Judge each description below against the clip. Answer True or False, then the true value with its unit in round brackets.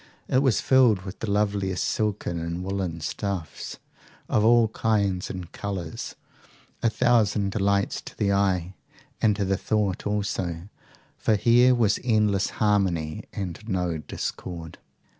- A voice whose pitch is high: False (100 Hz)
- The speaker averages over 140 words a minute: False (135 wpm)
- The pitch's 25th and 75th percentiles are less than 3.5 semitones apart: True (2.8 semitones)